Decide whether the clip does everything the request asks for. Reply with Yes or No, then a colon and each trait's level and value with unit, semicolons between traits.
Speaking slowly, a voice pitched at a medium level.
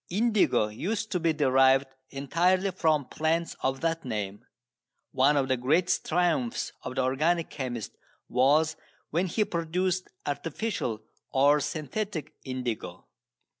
Yes: slow, 125 wpm; medium, 155 Hz